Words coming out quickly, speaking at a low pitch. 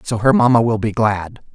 Yes: fast, 230 wpm; low, 115 Hz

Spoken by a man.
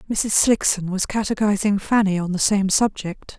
No: female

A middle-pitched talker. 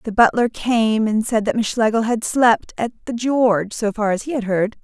No: high, 225 Hz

